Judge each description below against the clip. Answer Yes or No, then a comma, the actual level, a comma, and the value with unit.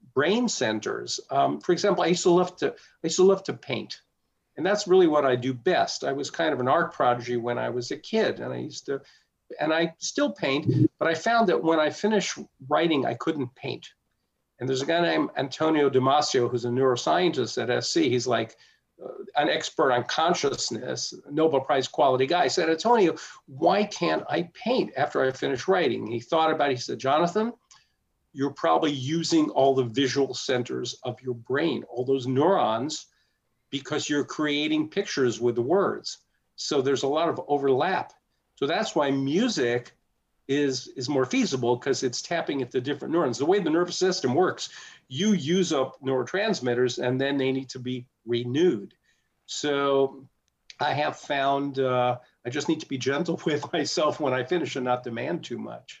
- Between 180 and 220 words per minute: Yes, average, 185 wpm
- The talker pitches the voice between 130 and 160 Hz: Yes, medium, 140 Hz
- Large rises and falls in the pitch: No, average, 4.9 semitones